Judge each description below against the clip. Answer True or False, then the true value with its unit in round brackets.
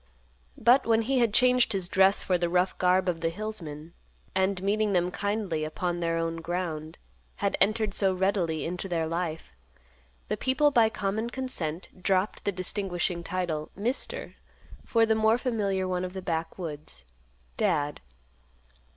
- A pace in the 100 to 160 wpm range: True (150 wpm)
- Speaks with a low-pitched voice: False (185 Hz)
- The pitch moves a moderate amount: True (4.3 semitones)